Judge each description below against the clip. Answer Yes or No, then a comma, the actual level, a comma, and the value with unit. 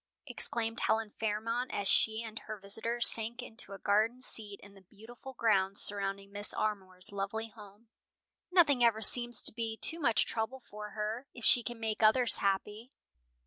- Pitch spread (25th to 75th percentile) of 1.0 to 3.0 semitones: Yes, narrow, 2.5 semitones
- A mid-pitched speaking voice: No, high, 220 Hz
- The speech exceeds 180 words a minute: No, average, 170 wpm